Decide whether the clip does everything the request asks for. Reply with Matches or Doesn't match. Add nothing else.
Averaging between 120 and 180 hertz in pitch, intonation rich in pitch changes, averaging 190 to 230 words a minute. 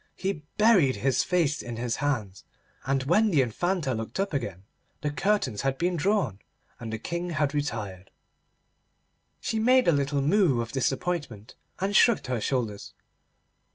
Doesn't match